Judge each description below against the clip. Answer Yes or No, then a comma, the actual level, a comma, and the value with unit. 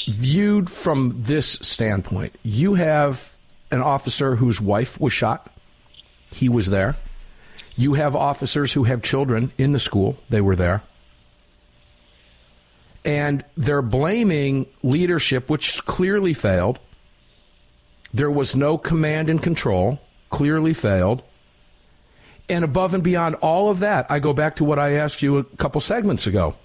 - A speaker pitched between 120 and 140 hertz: Yes, low, 135 Hz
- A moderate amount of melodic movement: No, wide, 7.8 semitones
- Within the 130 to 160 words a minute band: Yes, slow, 135 wpm